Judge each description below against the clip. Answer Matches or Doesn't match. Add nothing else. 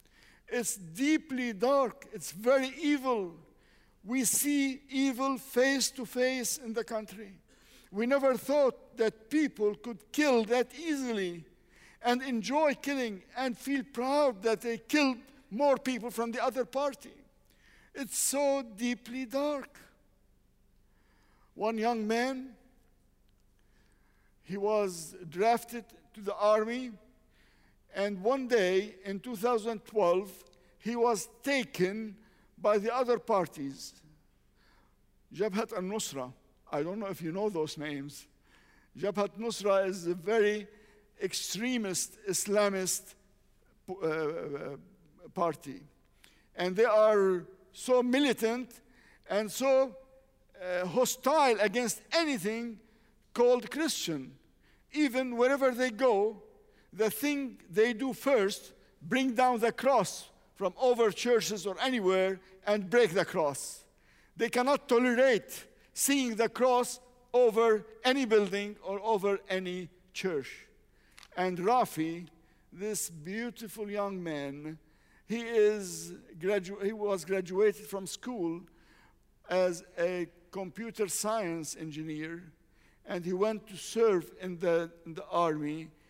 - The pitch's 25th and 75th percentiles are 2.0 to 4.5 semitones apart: Doesn't match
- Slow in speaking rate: Matches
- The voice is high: Matches